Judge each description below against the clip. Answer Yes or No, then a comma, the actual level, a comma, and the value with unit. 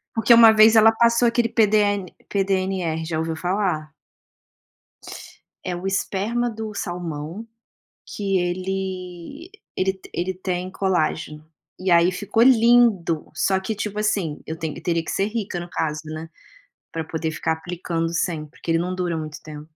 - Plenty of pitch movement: No, average, 4.2 semitones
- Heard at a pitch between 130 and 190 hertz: Yes, medium, 185 Hz